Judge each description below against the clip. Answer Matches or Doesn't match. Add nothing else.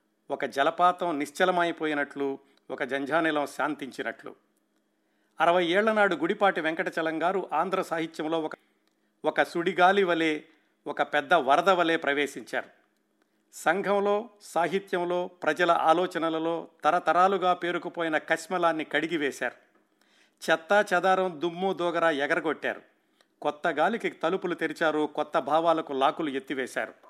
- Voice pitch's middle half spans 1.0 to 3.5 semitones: Matches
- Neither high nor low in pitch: Matches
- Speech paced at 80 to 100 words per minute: Matches